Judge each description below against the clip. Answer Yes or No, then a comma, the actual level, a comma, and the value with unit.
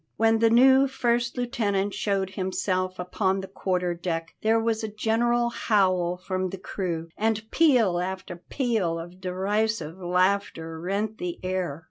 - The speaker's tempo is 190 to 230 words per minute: No, average, 145 wpm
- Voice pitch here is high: Yes, high, 195 Hz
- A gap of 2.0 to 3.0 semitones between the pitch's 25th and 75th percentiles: No, average, 3.6 semitones